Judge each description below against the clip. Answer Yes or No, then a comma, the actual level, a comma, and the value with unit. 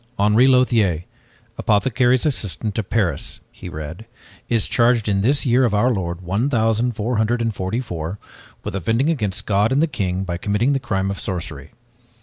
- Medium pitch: No, low, 110 Hz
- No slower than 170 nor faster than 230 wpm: Yes, average, 175 wpm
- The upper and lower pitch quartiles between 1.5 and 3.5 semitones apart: No, average, 4.2 semitones